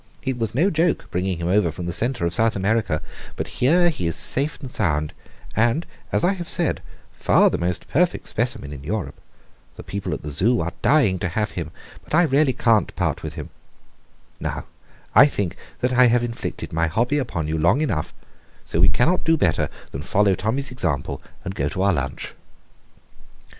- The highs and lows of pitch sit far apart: Yes, wide, 7.5 semitones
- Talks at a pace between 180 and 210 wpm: Yes, average, 195 wpm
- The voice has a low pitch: Yes, low, 110 Hz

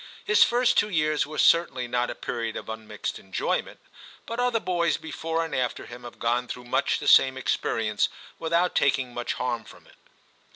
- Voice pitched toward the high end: No, low, 130 Hz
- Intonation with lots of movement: Yes, wide, 5.7 semitones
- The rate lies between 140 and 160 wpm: No, average, 190 wpm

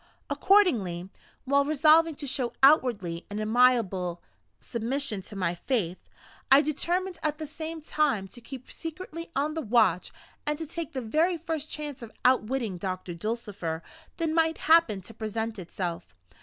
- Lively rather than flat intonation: Yes, wide, 7.3 semitones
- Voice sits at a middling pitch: No, very high, 255 Hz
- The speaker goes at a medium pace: Yes, average, 150 wpm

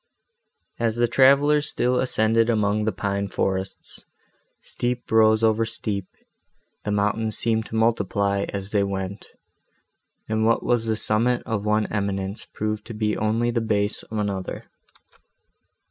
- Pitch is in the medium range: No, low, 110 Hz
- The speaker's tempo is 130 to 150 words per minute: Yes, average, 140 wpm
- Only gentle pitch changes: Yes, narrow, 2.1 semitones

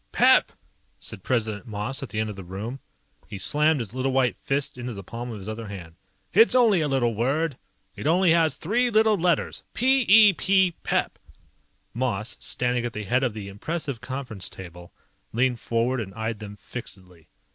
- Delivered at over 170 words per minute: Yes, average, 190 wpm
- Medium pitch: No, low, 125 Hz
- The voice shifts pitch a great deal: Yes, wide, 6.5 semitones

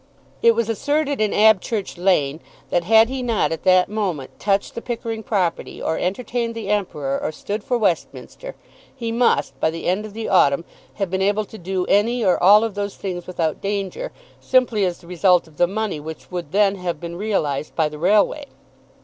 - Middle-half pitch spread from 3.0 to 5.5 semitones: Yes, average, 4.1 semitones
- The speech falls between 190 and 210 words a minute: Yes, average, 195 wpm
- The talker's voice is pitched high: Yes, high, 200 Hz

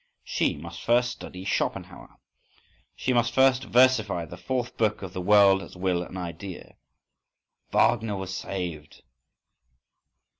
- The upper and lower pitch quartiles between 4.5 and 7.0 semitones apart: Yes, average, 5.0 semitones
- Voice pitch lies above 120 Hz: No, very low, 95 Hz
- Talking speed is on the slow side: Yes, slow, 125 wpm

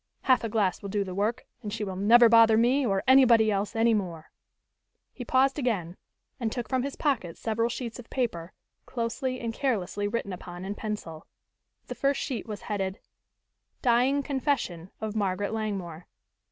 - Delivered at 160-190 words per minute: Yes, average, 170 wpm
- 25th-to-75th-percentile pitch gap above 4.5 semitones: No, average, 4.0 semitones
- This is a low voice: No, high, 220 Hz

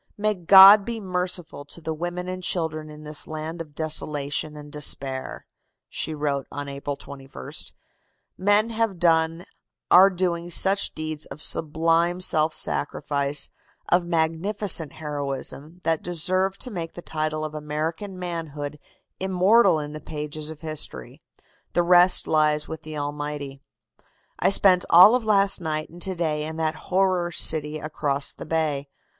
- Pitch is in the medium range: Yes, medium, 160 Hz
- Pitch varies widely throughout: No, average, 3.1 semitones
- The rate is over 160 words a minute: No, average, 150 wpm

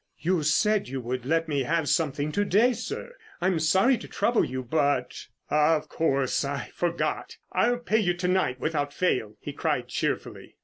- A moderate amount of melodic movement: Yes, average, 5.0 semitones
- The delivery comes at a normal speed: Yes, average, 175 wpm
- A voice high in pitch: No, medium, 160 Hz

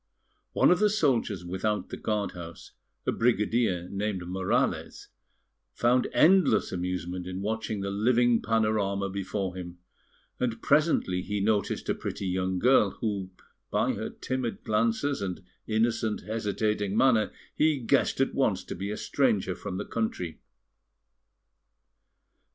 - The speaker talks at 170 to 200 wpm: No, slow, 135 wpm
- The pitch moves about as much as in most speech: Yes, average, 3.6 semitones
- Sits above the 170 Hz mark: No, low, 105 Hz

